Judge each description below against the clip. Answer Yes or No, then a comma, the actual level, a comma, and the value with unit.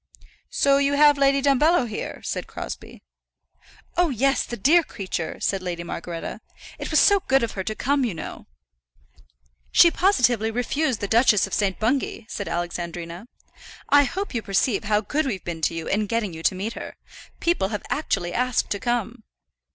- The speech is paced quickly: No, average, 175 wpm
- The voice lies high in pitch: Yes, high, 230 Hz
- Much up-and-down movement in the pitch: Yes, wide, 6.3 semitones